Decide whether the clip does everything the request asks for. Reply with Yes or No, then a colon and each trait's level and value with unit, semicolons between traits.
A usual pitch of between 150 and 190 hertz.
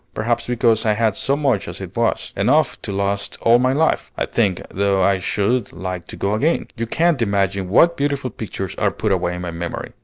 No: low, 105 Hz